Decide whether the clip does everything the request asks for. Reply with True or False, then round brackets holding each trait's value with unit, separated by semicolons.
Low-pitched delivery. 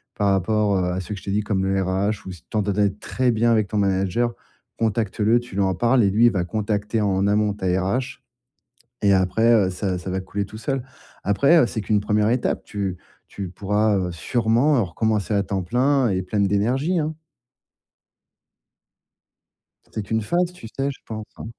True (105 Hz)